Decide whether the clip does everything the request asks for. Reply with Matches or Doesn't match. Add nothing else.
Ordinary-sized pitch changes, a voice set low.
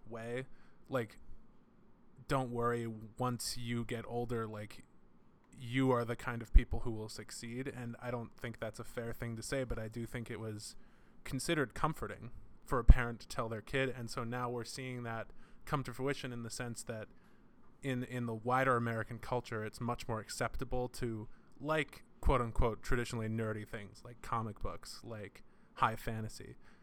Doesn't match